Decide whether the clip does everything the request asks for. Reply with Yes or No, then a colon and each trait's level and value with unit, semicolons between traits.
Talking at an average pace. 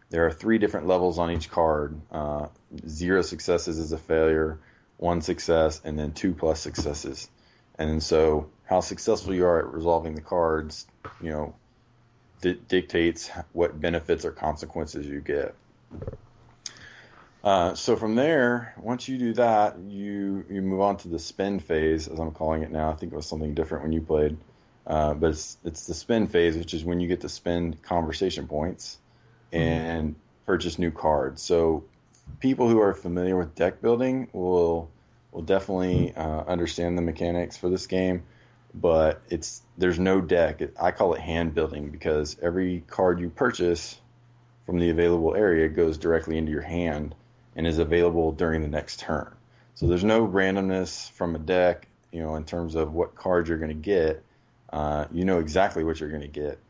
Yes: average, 175 wpm